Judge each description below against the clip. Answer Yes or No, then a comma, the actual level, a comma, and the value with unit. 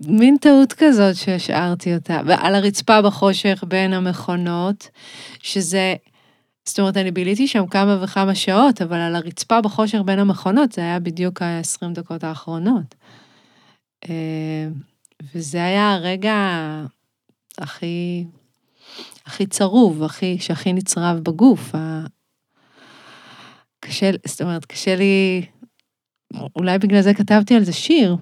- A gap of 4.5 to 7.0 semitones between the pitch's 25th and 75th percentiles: No, average, 3.0 semitones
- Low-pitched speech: No, medium, 185 Hz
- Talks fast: No, average, 115 wpm